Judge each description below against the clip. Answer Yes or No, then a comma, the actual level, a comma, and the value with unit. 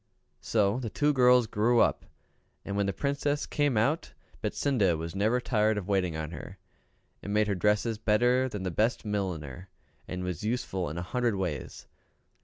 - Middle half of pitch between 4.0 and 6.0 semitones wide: Yes, average, 4.9 semitones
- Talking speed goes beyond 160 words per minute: Yes, average, 175 wpm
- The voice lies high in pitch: No, low, 105 Hz